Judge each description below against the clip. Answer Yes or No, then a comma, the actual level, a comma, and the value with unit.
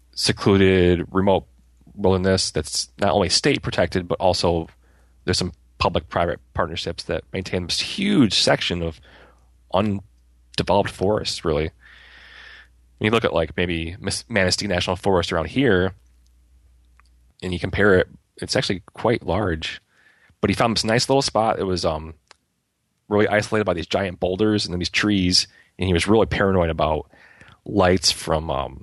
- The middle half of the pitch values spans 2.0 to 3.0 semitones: No, average, 5.1 semitones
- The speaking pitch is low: Yes, very low, 90 Hz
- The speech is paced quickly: No, average, 150 wpm